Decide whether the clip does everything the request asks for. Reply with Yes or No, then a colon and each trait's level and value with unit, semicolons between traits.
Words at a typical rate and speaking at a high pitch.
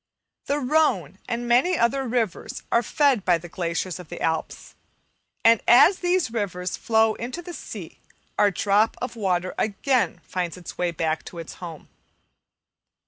Yes: average, 155 wpm; high, 215 Hz